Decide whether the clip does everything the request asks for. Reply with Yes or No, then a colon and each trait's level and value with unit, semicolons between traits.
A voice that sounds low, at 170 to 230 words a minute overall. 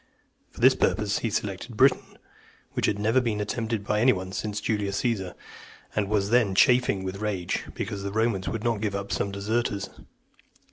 Yes: low, 105 Hz; average, 185 wpm